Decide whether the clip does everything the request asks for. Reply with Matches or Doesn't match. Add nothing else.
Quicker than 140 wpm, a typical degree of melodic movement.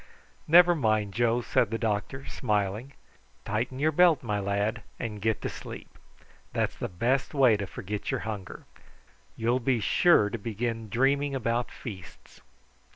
Matches